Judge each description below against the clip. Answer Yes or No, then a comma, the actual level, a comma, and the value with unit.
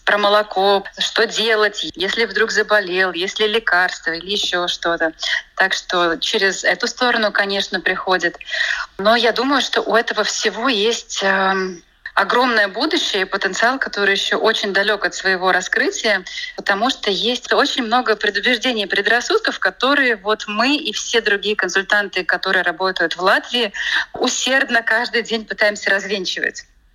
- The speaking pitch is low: No, high, 210 Hz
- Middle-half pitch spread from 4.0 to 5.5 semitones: No, average, 3.4 semitones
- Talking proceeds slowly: No, average, 140 wpm